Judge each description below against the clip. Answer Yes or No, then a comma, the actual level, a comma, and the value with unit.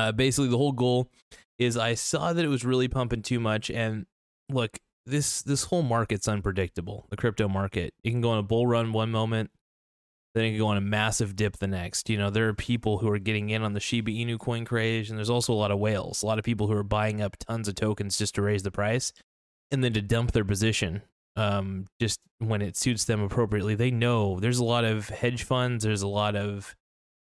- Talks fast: Yes, fast, 235 wpm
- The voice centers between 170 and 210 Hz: No, low, 110 Hz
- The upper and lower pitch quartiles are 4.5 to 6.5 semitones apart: No, narrow, 2.6 semitones